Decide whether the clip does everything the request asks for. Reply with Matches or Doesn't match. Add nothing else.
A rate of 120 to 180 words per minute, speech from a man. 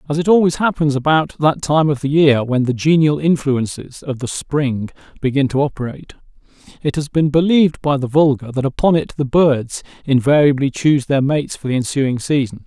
Doesn't match